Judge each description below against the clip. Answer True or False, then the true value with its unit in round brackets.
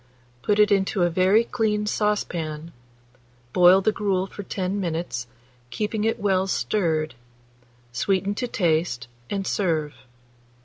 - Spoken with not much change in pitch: False (3.7 semitones)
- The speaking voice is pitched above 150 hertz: True (190 Hz)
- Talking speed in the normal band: False (125 wpm)